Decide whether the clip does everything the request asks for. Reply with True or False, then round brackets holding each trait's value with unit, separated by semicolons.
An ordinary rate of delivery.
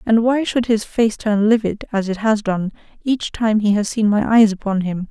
False (235 wpm)